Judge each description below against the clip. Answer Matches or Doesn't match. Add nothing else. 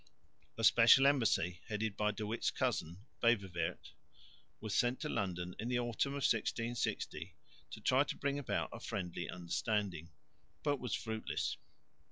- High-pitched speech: Doesn't match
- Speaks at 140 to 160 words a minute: Matches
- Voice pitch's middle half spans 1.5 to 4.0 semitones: Doesn't match